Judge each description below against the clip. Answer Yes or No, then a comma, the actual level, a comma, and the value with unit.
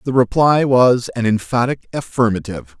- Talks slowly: Yes, slow, 130 wpm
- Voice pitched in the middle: No, low, 120 Hz